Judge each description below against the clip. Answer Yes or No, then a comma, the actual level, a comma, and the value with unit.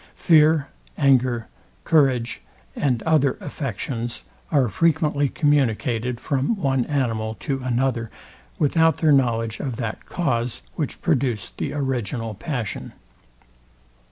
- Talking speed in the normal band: No, slow, 105 wpm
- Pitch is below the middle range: Yes, low, 130 Hz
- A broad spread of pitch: No, average, 3.9 semitones